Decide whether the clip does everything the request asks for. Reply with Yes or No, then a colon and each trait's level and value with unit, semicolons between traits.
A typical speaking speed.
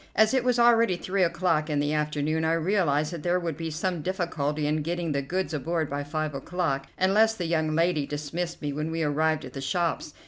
No: fast, 215 wpm